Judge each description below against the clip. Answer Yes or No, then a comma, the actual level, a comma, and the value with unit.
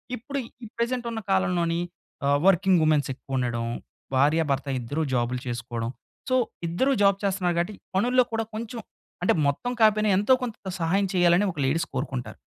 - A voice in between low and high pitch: Yes, medium, 175 Hz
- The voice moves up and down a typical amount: No, wide, 7.2 semitones